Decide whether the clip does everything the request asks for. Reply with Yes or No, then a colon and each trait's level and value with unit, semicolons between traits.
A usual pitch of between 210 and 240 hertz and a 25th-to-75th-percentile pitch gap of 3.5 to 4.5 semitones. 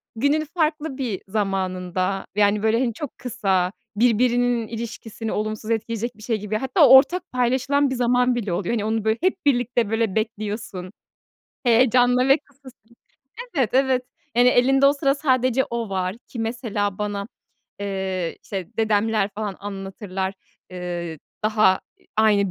Yes: high, 225 Hz; average, 3.8 semitones